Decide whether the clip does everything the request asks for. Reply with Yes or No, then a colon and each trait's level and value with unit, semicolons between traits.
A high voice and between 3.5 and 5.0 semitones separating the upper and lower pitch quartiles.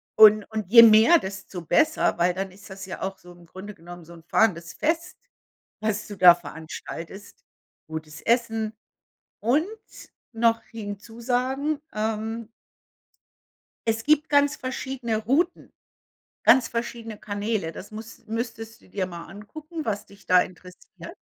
Yes: high, 215 Hz; average, 3.9 semitones